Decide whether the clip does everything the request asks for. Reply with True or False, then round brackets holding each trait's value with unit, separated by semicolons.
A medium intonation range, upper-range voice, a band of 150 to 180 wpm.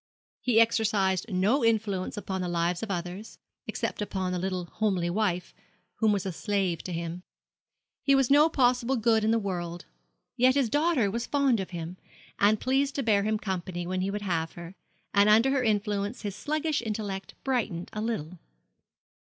True (4.2 semitones; 205 Hz; 175 wpm)